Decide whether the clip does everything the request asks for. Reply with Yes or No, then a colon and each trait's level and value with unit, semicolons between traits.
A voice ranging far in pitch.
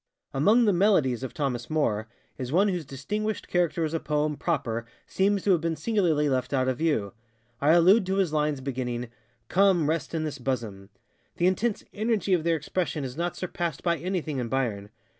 Yes: wide, 5.9 semitones